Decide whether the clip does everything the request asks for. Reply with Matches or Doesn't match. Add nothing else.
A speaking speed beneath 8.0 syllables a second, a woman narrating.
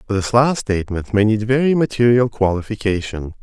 Doesn't match